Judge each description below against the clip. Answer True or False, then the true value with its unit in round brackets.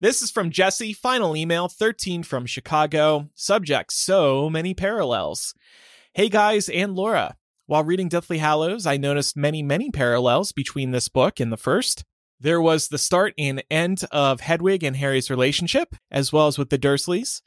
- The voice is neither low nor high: True (160 Hz)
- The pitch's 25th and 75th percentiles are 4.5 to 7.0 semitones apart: True (5.4 semitones)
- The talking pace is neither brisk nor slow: True (170 wpm)